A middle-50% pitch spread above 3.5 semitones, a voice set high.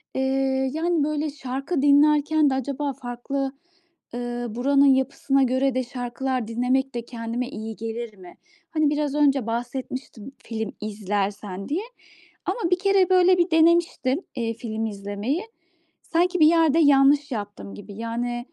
Yes: average, 4.2 semitones; very high, 265 Hz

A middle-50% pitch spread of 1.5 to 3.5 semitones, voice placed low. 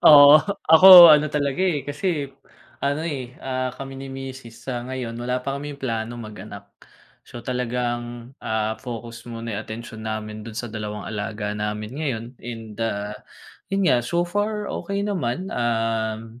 No: average, 4.2 semitones; low, 120 Hz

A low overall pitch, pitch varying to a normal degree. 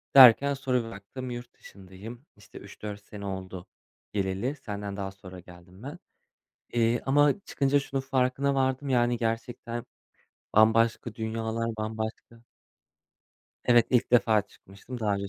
Yes: low, 115 Hz; average, 4.0 semitones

